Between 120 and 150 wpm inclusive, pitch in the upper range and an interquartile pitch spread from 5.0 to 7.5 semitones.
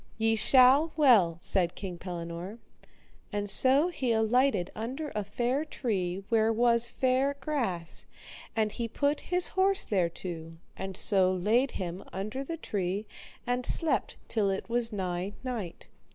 Yes: average, 140 wpm; high, 220 Hz; wide, 5.6 semitones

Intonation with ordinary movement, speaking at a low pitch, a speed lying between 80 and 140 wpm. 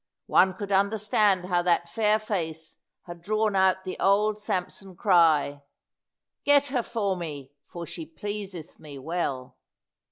No: average, 3.9 semitones; medium, 185 Hz; slow, 135 wpm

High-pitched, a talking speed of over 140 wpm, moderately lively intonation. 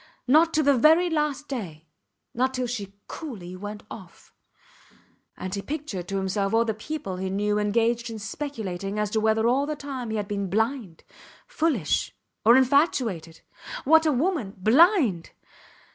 No: high, 225 Hz; average, 160 wpm; wide, 6.1 semitones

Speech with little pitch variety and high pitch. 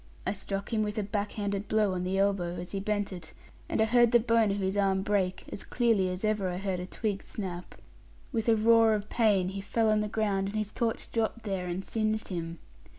Yes: narrow, 2.3 semitones; high, 205 Hz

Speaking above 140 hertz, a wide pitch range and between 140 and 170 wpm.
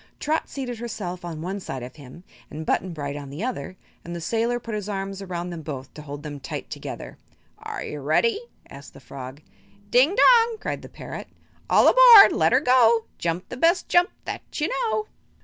No: high, 190 Hz; wide, 9.0 semitones; average, 200 wpm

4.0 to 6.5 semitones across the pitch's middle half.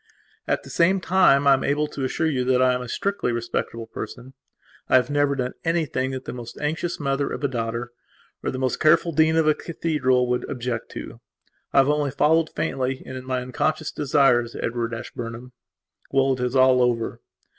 No: average, 3.1 semitones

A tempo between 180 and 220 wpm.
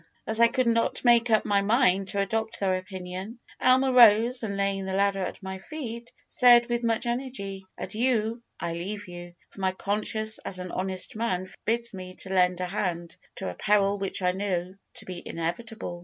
Yes: average, 190 wpm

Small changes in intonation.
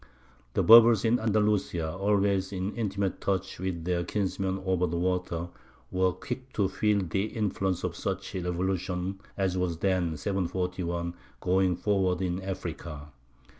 Yes: narrow, 1.9 semitones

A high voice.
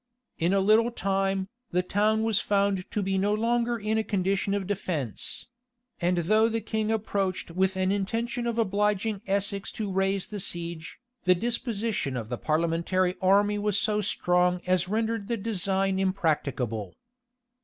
Yes: high, 195 Hz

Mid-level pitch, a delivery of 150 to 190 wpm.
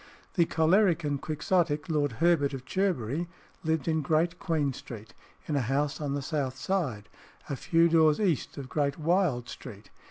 Yes: medium, 155 Hz; average, 165 wpm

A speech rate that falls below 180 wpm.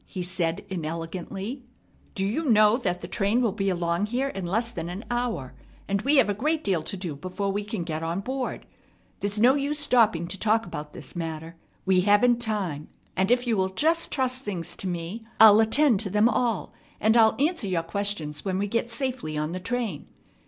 No: average, 200 wpm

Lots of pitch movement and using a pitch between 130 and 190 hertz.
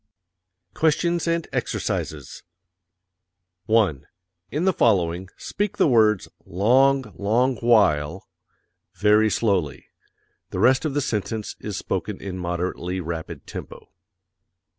No: wide, 6.3 semitones; low, 105 Hz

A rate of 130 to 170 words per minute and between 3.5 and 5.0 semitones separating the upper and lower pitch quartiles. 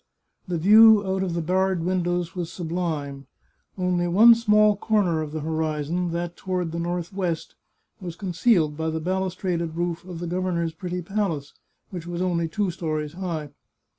No: average, 160 wpm; narrow, 2.4 semitones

